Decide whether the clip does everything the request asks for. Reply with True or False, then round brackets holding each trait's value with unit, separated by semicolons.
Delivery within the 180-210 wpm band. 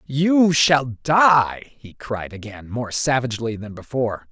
False (140 wpm)